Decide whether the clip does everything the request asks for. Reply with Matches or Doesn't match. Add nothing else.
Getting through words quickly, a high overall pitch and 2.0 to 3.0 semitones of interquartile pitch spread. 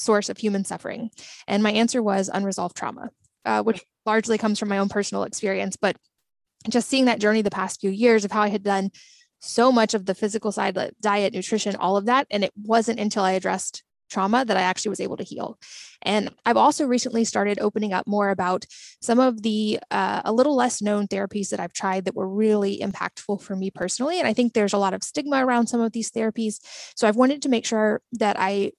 Matches